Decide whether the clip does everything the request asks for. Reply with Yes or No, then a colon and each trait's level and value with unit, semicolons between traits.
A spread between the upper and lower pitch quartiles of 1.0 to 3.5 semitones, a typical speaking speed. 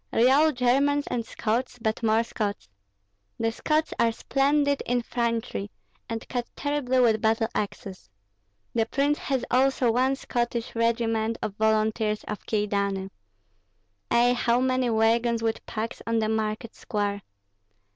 No: narrow, 2.4 semitones; slow, 130 wpm